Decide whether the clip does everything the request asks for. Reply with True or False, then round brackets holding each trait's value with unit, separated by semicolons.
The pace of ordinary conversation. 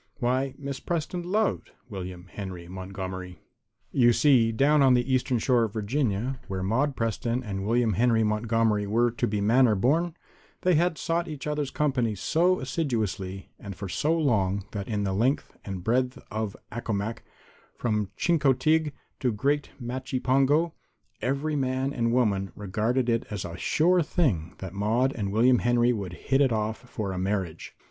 True (160 wpm)